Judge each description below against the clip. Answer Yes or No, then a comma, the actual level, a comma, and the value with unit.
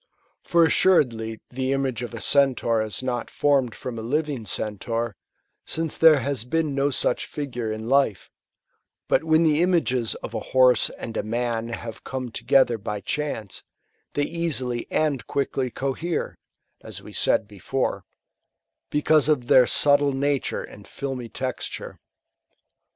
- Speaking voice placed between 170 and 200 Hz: No, low, 130 Hz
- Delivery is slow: No, average, 145 wpm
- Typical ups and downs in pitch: Yes, average, 3.8 semitones